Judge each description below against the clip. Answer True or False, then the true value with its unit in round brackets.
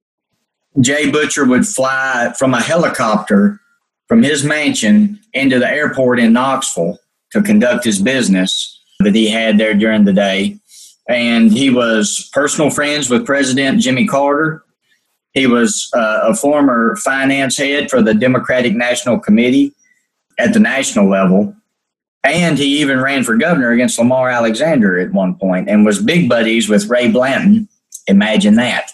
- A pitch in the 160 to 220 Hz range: False (140 Hz)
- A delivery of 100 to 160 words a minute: True (150 wpm)